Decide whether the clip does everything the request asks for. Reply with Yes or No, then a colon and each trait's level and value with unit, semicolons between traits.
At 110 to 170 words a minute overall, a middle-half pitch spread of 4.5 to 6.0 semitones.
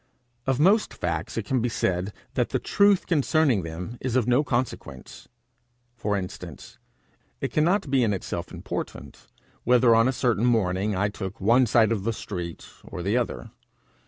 Yes: average, 165 wpm; average, 5.2 semitones